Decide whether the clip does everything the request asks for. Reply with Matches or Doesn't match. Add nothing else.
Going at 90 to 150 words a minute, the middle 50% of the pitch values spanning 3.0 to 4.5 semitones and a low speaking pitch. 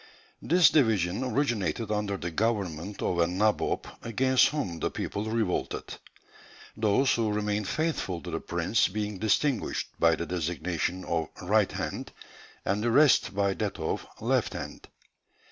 Matches